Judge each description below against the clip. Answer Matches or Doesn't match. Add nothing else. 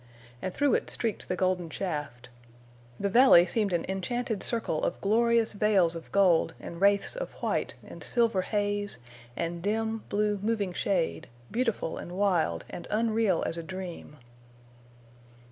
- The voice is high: Matches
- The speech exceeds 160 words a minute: Doesn't match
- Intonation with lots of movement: Doesn't match